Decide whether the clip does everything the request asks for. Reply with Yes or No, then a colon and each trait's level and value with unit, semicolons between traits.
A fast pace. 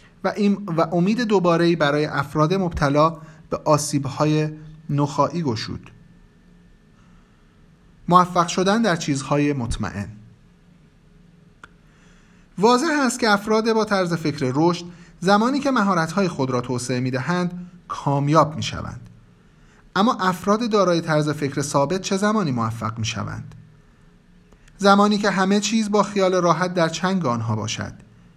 No: average, 120 wpm